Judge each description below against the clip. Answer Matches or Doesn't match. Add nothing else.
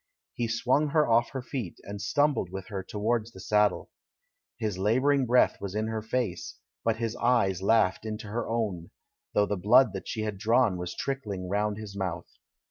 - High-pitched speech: Doesn't match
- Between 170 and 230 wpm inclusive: Matches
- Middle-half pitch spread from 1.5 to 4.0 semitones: Matches